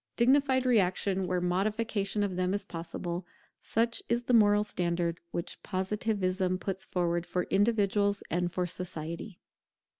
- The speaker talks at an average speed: No, slow, 130 wpm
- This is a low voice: No, high, 190 Hz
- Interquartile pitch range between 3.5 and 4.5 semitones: No, average, 3.0 semitones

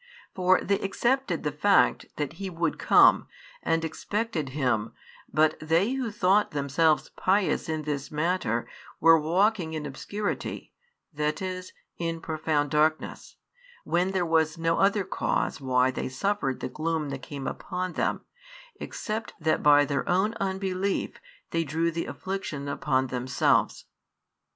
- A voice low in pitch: No, medium, 165 Hz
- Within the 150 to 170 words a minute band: No, average, 140 wpm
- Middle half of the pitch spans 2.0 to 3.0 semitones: No, average, 4.3 semitones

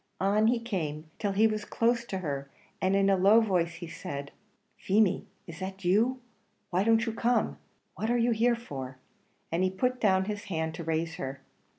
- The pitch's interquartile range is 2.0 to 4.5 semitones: No, average, 5.1 semitones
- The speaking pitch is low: No, high, 195 Hz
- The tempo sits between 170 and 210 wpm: Yes, average, 195 wpm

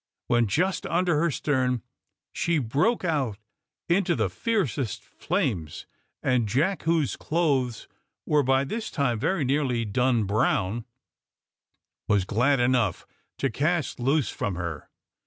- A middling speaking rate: No, slow, 125 wpm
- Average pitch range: No, wide, 5.8 semitones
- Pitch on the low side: Yes, low, 130 Hz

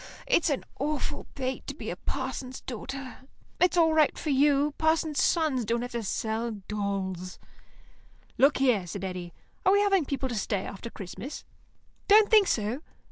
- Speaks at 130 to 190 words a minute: Yes, average, 165 wpm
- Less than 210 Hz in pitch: No, very high, 265 Hz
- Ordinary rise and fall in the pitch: No, wide, 6.2 semitones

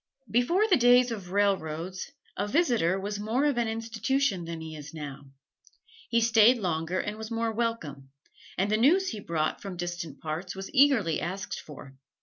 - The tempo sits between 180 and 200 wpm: No, average, 170 wpm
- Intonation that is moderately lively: No, wide, 5.9 semitones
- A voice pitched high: Yes, high, 205 Hz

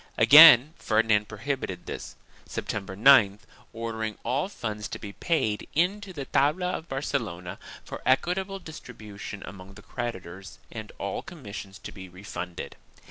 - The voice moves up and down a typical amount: No, wide, 6.4 semitones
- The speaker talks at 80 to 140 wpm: Yes, slow, 135 wpm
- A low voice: Yes, low, 110 Hz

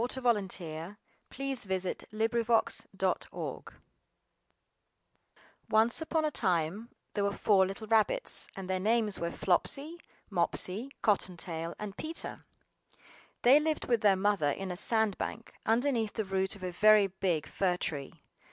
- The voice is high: Yes, high, 205 Hz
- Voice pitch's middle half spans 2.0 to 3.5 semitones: No, average, 3.9 semitones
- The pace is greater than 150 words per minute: No, average, 145 wpm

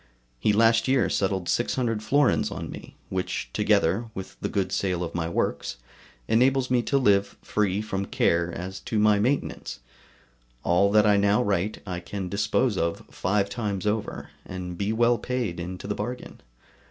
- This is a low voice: Yes, low, 100 Hz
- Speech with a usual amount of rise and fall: Yes, average, 3.6 semitones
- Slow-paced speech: No, average, 165 wpm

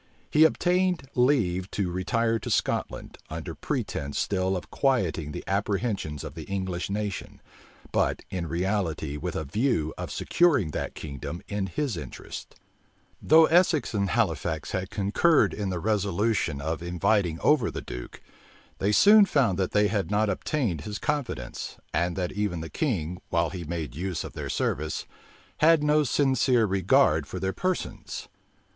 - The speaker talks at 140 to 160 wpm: Yes, average, 155 wpm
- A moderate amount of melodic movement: No, wide, 6.3 semitones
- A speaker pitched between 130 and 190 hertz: No, low, 100 Hz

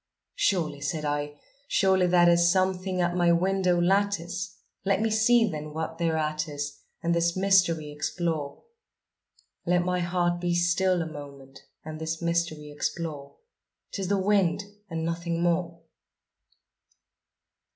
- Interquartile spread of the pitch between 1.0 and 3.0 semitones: Yes, average, 2.7 semitones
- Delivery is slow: Yes, slow, 130 wpm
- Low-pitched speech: No, medium, 170 Hz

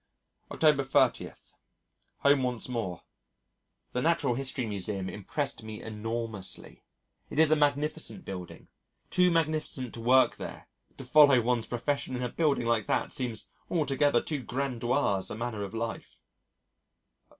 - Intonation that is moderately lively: Yes, average, 4.2 semitones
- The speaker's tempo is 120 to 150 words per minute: Yes, slow, 135 wpm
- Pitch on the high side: No, low, 125 Hz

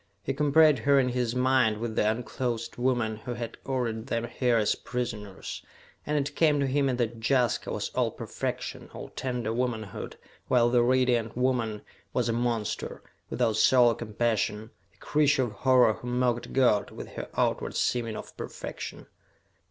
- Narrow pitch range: Yes, narrow, 2.3 semitones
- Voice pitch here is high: No, low, 120 Hz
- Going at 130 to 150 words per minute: No, average, 165 wpm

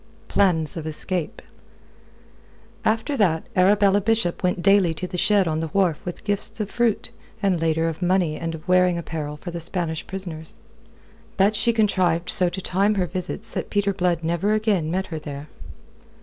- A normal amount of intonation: Yes, average, 3.5 semitones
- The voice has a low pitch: No, medium, 180 Hz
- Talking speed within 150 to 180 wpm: Yes, average, 175 wpm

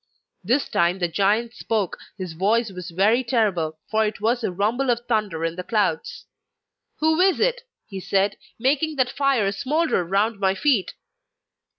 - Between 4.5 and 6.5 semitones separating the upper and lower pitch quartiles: Yes, average, 4.8 semitones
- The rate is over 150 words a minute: Yes, average, 165 wpm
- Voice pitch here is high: Yes, high, 215 Hz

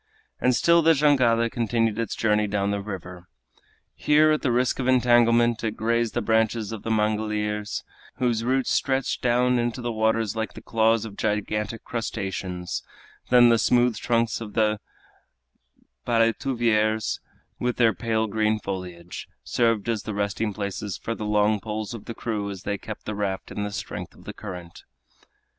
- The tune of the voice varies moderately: No, narrow, 2.2 semitones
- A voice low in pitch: Yes, low, 110 Hz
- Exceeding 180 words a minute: No, average, 165 wpm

